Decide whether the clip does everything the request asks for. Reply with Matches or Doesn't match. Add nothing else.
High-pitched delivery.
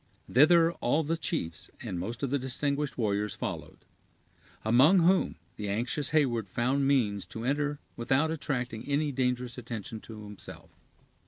Doesn't match